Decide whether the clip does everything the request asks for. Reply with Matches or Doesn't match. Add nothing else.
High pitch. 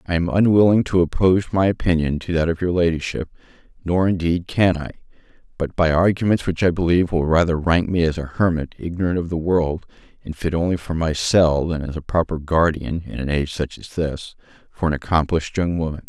Doesn't match